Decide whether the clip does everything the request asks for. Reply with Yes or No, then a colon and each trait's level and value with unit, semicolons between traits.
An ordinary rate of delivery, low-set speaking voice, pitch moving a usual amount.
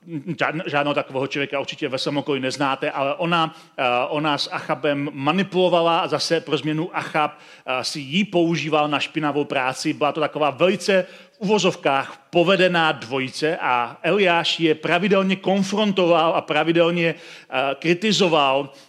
No: average, 125 wpm; medium, 155 Hz; average, 3.2 semitones